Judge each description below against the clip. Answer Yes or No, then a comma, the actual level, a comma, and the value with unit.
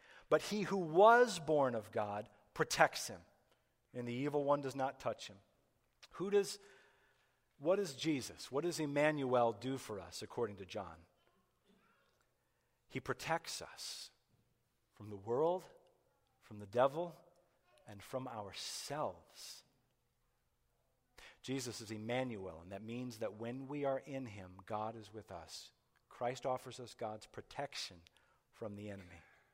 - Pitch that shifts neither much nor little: No, wide, 5.7 semitones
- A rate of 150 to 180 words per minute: No, slow, 135 wpm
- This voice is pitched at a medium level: No, low, 125 Hz